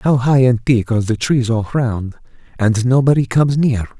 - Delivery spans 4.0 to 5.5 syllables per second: Yes, 5.0 syllables/s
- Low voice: Yes, low, 125 Hz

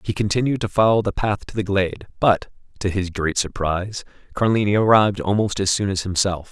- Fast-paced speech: No, average, 195 wpm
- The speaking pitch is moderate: No, low, 100 Hz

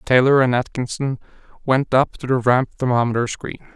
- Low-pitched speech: Yes, low, 130 Hz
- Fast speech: No, average, 160 wpm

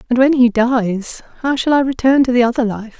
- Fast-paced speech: Yes, fast, 240 wpm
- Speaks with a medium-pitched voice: No, high, 245 Hz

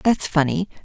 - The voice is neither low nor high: Yes, medium, 170 Hz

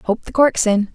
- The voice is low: No, high, 225 Hz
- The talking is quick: Yes, fast, 255 wpm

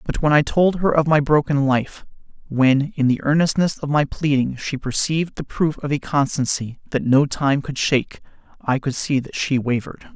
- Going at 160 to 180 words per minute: No, average, 195 wpm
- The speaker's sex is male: Yes, male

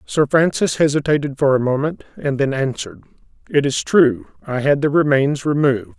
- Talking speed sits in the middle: Yes, average, 170 wpm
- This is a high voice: No, medium, 140 Hz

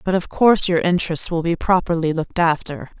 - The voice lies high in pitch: No, medium, 170 Hz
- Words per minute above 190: Yes, average, 200 wpm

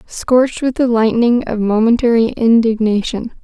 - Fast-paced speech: No, slow, 120 wpm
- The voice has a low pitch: No, high, 230 Hz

